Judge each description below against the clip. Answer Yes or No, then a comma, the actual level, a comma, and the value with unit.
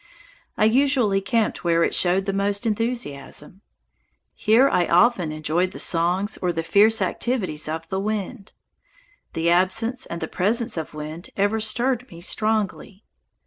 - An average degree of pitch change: Yes, average, 4.7 semitones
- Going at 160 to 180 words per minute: No, average, 145 wpm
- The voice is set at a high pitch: Yes, high, 195 Hz